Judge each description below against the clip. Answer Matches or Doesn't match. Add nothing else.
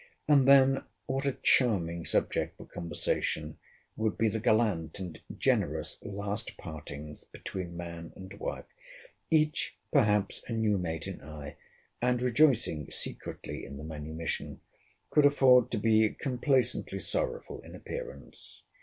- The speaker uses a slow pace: Matches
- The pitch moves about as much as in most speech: Doesn't match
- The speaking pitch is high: Doesn't match